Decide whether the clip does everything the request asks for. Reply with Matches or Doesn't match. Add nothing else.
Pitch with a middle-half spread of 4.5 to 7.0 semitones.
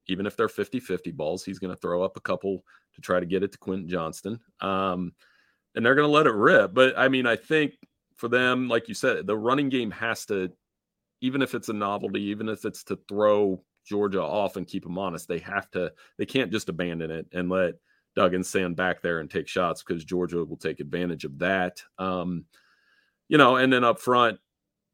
Matches